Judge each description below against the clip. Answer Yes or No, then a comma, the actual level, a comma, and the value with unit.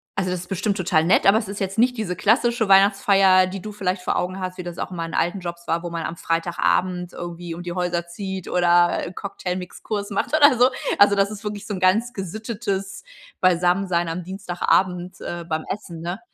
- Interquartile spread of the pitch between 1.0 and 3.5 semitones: Yes, narrow, 2.4 semitones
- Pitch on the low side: No, medium, 185 Hz